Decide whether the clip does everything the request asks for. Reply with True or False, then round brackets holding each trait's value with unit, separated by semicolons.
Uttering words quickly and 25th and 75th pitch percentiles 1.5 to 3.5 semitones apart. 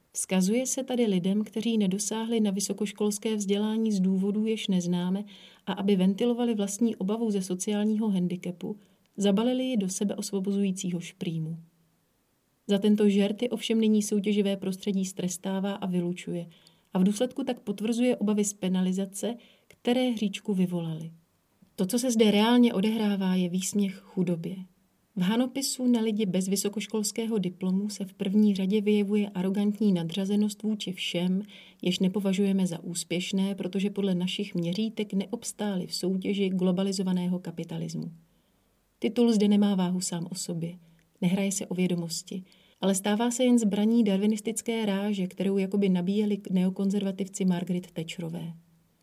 False (135 wpm; 2.5 semitones)